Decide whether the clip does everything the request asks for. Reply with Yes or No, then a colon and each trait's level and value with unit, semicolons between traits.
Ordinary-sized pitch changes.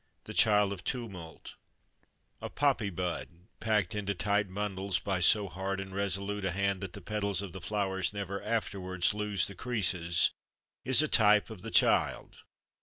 No: narrow, 2.0 semitones